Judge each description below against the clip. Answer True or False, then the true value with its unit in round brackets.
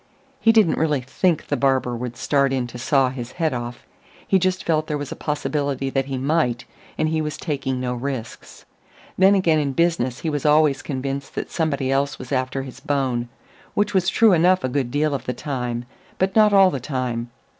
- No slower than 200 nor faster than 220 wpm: True (205 wpm)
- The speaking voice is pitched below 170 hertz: True (140 Hz)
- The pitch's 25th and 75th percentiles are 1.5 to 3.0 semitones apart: False (3.7 semitones)